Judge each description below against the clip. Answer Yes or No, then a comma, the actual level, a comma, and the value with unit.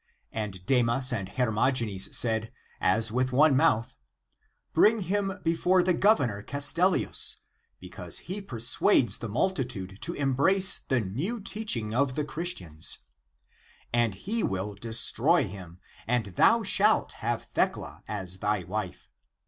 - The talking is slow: Yes, slow, 130 wpm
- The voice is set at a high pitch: No, low, 125 Hz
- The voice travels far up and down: Yes, wide, 8.5 semitones